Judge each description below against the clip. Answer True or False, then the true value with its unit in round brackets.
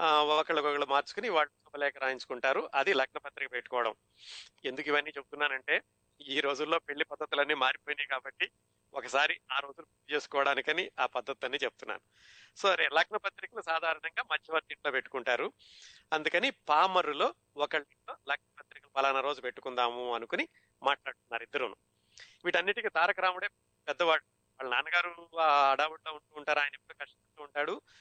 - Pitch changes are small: True (2.3 semitones)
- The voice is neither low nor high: True (145 Hz)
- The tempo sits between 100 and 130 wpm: True (120 wpm)